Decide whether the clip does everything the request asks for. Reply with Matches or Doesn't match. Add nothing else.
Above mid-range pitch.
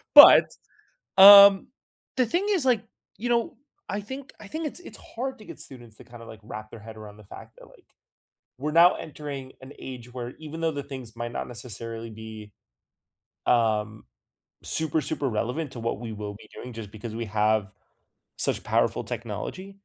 Doesn't match